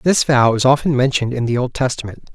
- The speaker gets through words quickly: Yes, fast, 230 wpm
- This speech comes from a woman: No, male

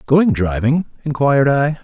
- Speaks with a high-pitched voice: No, medium, 140 Hz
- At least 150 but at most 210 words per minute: No, slow, 130 wpm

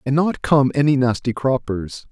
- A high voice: No, low, 130 Hz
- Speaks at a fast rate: No, average, 170 wpm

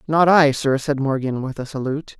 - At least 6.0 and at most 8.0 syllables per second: No, 5.4 syllables/s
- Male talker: Yes, male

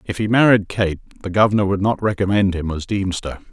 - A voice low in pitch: Yes, low, 100 Hz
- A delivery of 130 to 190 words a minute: No, fast, 205 wpm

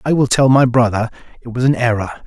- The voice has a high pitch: No, low, 120 Hz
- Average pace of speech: No, fast, 240 wpm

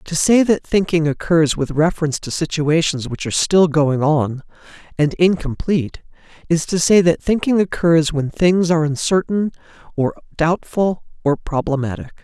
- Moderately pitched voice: Yes, medium, 160 Hz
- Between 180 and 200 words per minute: No, average, 145 wpm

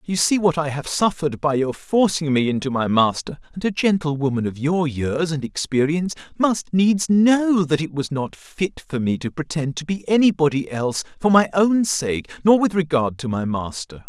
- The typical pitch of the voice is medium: Yes, medium, 160 Hz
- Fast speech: Yes, fast, 210 wpm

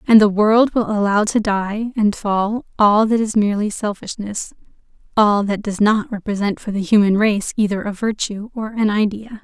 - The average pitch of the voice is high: Yes, high, 210 Hz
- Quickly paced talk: No, average, 185 wpm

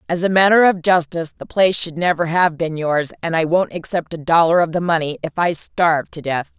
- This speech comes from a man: No, female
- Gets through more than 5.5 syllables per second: Yes, 5.7 syllables/s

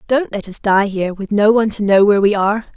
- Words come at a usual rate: No, fast, 285 wpm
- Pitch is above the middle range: Yes, high, 205 Hz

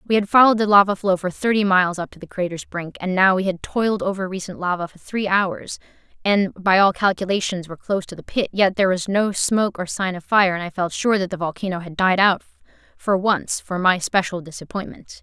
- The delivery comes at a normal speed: No, fast, 235 wpm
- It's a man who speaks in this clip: No, female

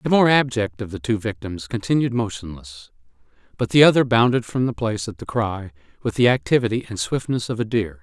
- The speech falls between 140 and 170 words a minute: No, average, 200 wpm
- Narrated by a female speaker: No, male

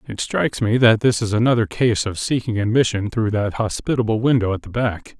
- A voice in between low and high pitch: No, low, 110 Hz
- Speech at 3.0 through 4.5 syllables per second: No, 5.6 syllables/s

